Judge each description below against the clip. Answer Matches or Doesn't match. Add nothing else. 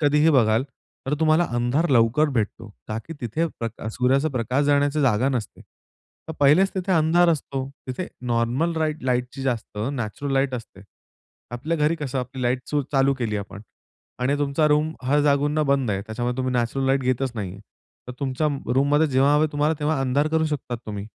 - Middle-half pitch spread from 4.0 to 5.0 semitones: Doesn't match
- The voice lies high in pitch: Doesn't match